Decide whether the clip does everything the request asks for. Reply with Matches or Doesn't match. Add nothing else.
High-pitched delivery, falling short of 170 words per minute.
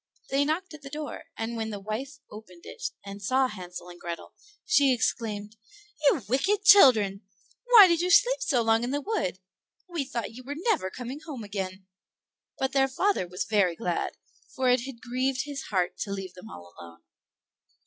Doesn't match